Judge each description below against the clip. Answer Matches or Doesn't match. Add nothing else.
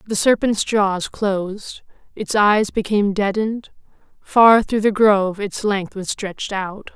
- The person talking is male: Doesn't match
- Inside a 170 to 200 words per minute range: Doesn't match